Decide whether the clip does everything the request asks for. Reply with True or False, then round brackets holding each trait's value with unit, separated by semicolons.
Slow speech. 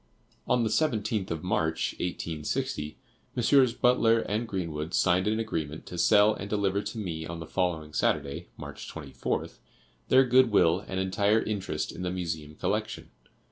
False (155 wpm)